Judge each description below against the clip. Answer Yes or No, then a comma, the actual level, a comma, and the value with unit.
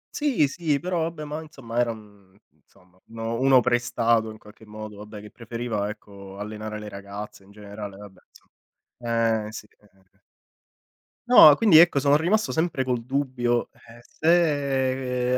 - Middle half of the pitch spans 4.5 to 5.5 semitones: Yes, average, 5.2 semitones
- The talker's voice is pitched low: Yes, low, 120 Hz